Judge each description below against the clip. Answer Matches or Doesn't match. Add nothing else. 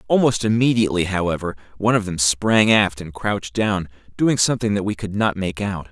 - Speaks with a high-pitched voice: Doesn't match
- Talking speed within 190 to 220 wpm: Matches